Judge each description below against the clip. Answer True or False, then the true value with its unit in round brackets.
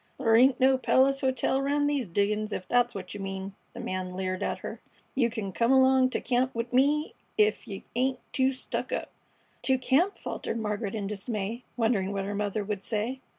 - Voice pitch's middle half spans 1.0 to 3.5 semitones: False (4.5 semitones)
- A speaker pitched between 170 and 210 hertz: False (230 Hz)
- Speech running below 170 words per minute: False (195 wpm)